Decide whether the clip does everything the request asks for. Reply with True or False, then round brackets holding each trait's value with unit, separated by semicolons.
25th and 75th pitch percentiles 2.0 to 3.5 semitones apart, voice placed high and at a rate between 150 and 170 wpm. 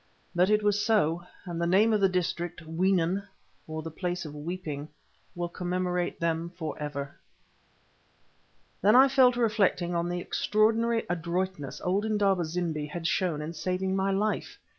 False (3.1 semitones; 180 Hz; 160 wpm)